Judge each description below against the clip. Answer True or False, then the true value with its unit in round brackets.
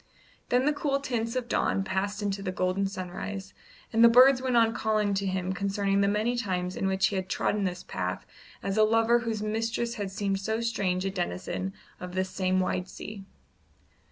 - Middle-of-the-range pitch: False (200 Hz)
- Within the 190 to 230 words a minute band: True (195 wpm)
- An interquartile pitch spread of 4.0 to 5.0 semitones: False (3.2 semitones)